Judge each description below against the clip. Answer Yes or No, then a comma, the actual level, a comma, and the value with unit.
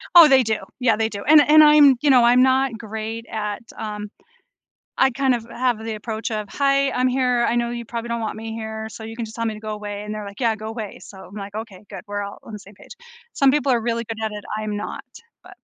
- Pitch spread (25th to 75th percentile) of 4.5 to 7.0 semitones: No, average, 2.8 semitones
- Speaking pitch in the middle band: No, high, 225 Hz